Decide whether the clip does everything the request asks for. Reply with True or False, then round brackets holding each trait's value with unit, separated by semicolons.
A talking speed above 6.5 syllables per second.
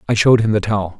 True (8.6 syllables/s)